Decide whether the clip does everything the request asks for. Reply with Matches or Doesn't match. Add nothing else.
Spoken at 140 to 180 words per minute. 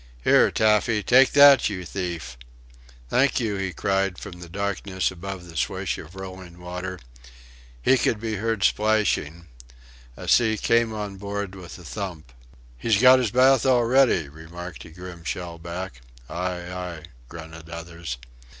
Matches